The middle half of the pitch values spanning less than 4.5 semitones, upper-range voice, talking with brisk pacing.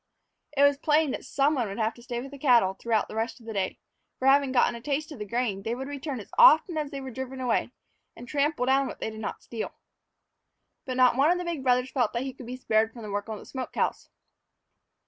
Yes: average, 3.4 semitones; very high, 255 Hz; fast, 260 wpm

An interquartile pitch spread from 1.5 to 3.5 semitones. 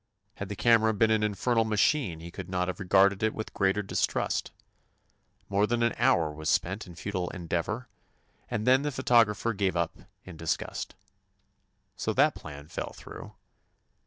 No: average, 4.1 semitones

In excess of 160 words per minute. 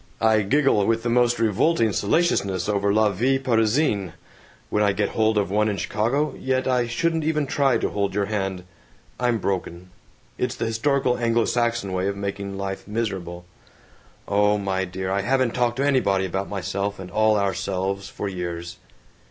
Yes: average, 175 wpm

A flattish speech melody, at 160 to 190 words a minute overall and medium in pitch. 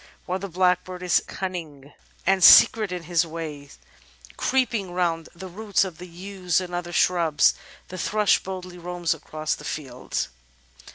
No: narrow, 2.2 semitones; average, 150 wpm; medium, 180 Hz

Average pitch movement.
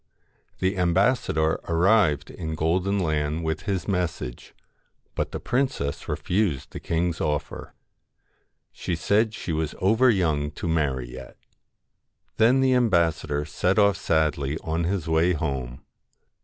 Yes: average, 4.4 semitones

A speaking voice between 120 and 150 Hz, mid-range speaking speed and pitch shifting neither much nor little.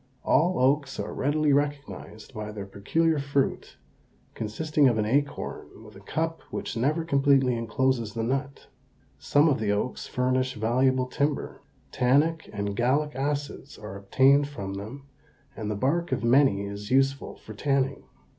Yes: low, 135 Hz; average, 150 wpm; average, 4.3 semitones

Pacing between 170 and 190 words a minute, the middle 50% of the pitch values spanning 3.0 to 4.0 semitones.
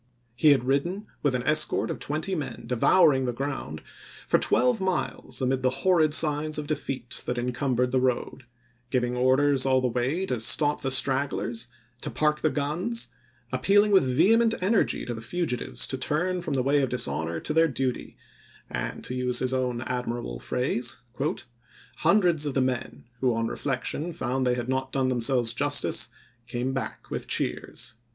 Yes: average, 175 wpm; average, 3.5 semitones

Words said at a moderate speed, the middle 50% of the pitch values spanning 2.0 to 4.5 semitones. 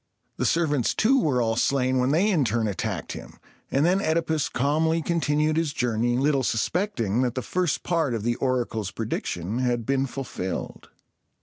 No: average, 170 wpm; average, 5.1 semitones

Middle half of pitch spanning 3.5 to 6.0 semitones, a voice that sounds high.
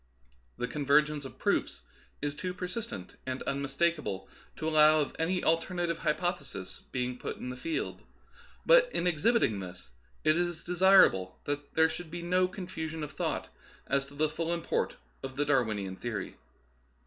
No: average, 4.7 semitones; medium, 155 Hz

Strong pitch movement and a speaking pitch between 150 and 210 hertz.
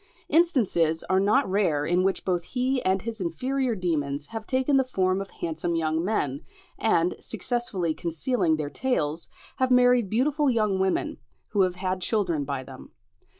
Yes: wide, 6.9 semitones; high, 190 Hz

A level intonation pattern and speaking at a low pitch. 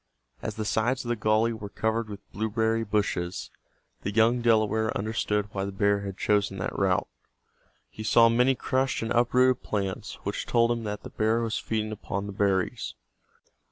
Yes: narrow, 2.2 semitones; low, 110 Hz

